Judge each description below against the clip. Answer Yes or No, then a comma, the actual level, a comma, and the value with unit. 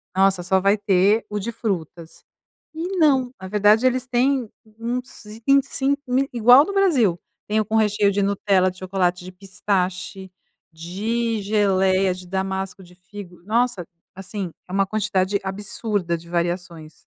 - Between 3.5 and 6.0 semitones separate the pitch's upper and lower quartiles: Yes, average, 3.8 semitones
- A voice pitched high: Yes, high, 200 Hz